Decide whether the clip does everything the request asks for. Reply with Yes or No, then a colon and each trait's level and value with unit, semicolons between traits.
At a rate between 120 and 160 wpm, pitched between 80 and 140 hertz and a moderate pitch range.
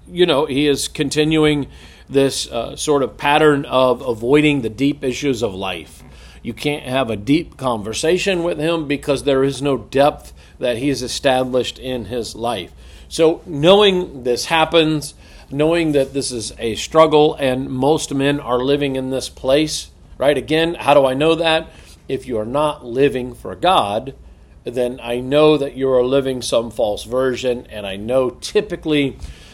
No: average, 170 wpm; low, 135 Hz; average, 3.3 semitones